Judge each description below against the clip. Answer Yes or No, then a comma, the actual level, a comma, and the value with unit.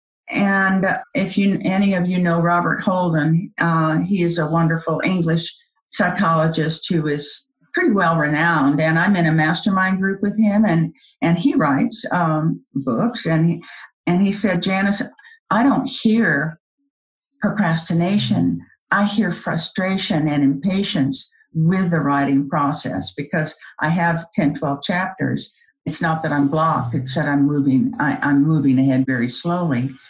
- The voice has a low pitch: No, medium, 170 Hz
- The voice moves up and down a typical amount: Yes, average, 4.3 semitones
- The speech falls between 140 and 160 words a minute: Yes, average, 150 wpm